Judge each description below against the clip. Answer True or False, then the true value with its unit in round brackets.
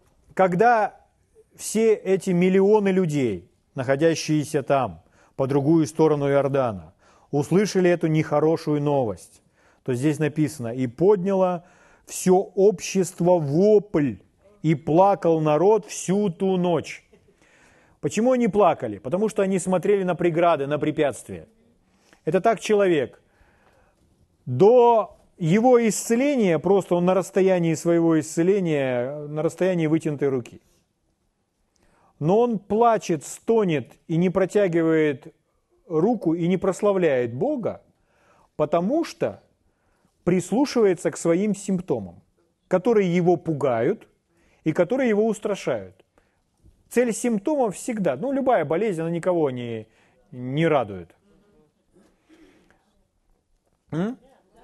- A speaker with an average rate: False (100 wpm)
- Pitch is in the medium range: True (175 Hz)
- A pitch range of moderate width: True (4.9 semitones)